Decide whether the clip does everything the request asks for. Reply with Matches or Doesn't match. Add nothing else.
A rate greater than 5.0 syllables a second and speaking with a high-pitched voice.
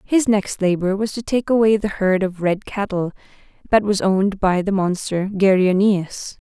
Doesn't match